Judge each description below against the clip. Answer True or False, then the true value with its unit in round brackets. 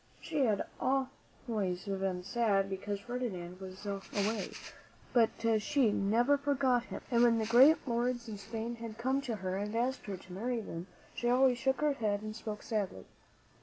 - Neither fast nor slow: True (170 wpm)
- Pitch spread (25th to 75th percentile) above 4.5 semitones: False (3.6 semitones)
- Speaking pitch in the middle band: False (225 Hz)